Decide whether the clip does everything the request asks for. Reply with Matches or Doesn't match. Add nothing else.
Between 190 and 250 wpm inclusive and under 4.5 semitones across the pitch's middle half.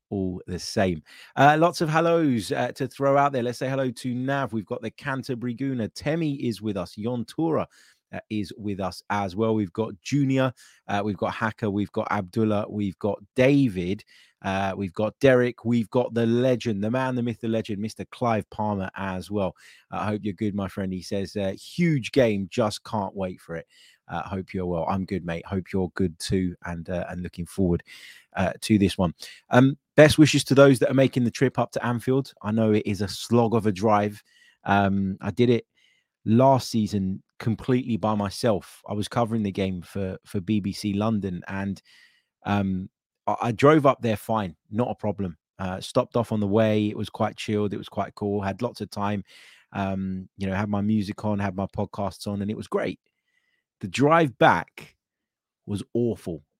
Matches